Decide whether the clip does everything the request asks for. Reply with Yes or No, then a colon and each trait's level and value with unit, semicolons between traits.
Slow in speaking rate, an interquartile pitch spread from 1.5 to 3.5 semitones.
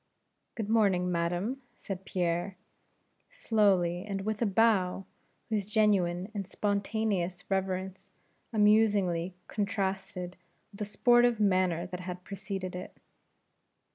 Yes: slow, 110 wpm; narrow, 2.6 semitones